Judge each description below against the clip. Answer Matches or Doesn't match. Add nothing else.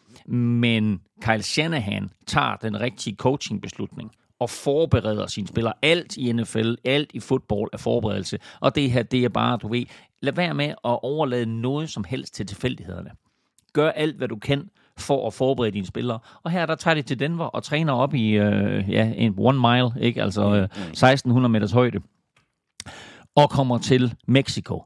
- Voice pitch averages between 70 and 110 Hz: Doesn't match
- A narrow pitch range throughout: Doesn't match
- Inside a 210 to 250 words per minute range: Doesn't match